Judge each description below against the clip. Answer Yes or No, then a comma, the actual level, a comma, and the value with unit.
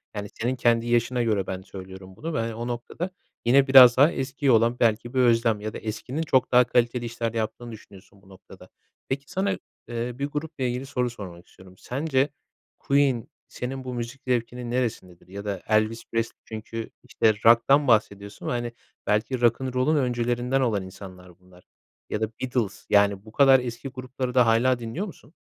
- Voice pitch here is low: Yes, low, 120 Hz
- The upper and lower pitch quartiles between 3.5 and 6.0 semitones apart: No, average, 3.0 semitones